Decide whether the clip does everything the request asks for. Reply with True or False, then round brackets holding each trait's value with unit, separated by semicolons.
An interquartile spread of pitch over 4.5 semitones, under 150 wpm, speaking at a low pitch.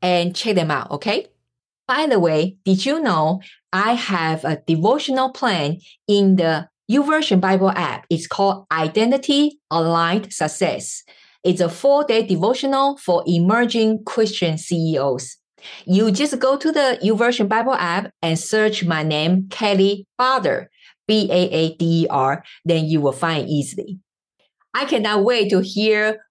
False (5.0 semitones; 135 wpm; 190 Hz)